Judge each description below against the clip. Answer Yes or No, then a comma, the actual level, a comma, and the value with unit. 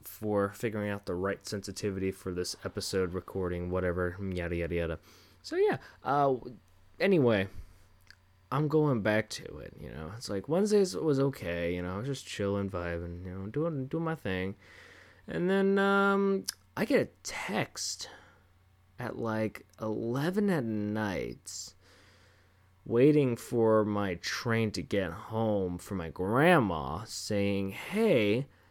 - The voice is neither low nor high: No, low, 100 Hz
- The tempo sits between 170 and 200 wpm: No, average, 145 wpm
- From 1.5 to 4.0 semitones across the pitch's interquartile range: No, average, 4.5 semitones